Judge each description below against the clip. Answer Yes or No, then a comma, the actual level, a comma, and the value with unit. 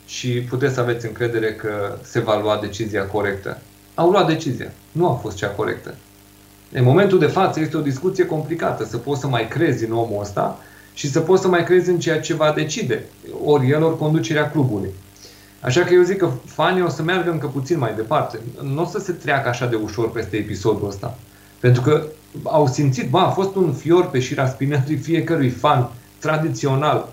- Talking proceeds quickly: Yes, fast, 200 wpm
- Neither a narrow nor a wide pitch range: No, wide, 6.3 semitones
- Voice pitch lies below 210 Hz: Yes, low, 135 Hz